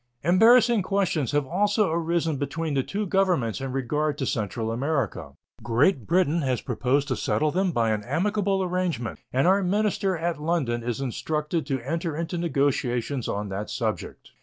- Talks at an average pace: Yes, average, 160 wpm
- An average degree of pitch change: No, wide, 5.8 semitones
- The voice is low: No, medium, 155 Hz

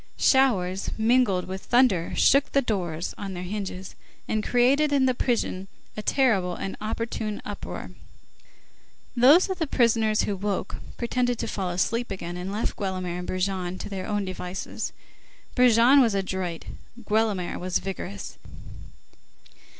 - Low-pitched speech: No, high, 205 Hz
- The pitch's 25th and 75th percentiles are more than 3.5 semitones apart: Yes, average, 4.6 semitones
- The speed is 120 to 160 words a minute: Yes, average, 140 wpm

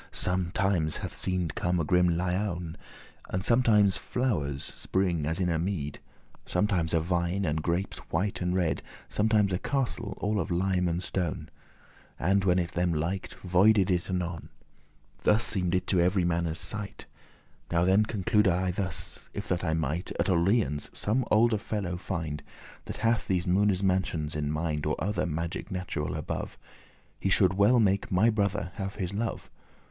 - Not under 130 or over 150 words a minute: No, average, 165 wpm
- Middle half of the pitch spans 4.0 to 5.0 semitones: No, average, 2.9 semitones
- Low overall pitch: Yes, very low, 90 Hz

